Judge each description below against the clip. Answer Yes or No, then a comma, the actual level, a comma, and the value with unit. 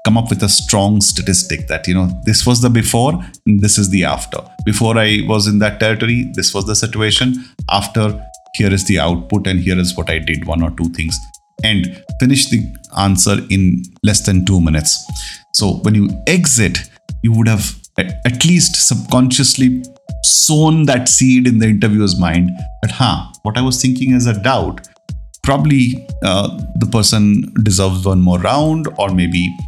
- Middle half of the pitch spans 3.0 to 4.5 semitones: No, average, 5.0 semitones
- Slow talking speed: No, average, 180 wpm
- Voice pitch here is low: Yes, low, 105 Hz